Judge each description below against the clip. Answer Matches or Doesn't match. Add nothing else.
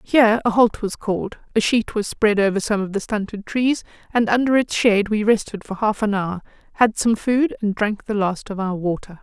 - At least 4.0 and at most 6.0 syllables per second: Matches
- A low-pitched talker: Doesn't match